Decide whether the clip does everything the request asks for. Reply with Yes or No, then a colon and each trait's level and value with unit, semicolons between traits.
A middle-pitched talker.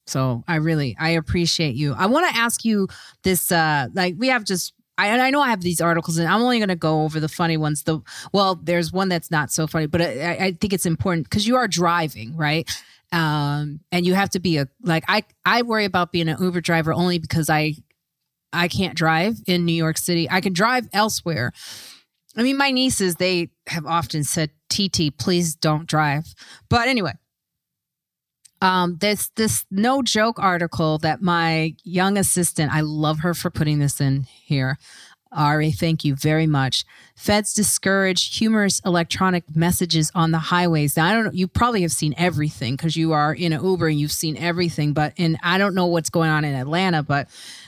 Yes: medium, 170 Hz